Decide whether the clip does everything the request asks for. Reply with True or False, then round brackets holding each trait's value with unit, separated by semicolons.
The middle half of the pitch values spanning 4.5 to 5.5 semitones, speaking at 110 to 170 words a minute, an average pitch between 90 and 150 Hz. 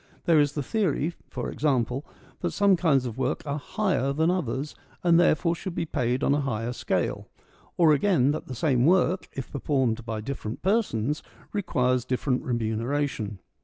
True (5.1 semitones; 165 wpm; 140 Hz)